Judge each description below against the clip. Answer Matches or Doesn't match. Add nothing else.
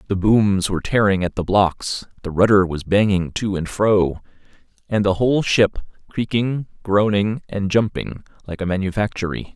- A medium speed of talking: Matches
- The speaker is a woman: Doesn't match